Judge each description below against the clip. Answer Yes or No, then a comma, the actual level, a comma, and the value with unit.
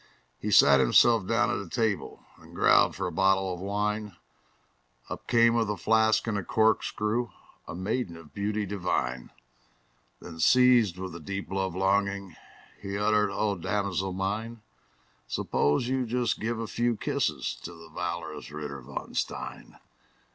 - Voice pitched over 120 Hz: No, low, 100 Hz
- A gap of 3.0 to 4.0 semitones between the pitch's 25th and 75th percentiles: Yes, average, 3.4 semitones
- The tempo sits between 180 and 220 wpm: No, average, 155 wpm